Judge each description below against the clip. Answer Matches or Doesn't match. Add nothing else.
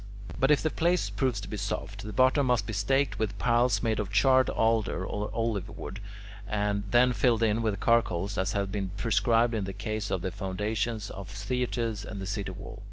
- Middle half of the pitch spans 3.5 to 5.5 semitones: Doesn't match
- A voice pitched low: Matches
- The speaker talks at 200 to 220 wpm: Matches